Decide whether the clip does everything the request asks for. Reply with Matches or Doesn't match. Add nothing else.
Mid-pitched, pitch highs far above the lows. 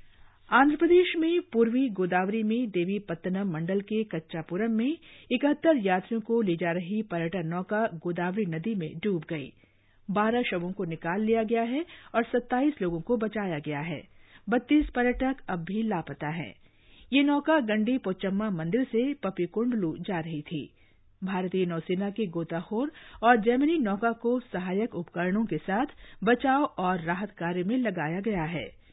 Doesn't match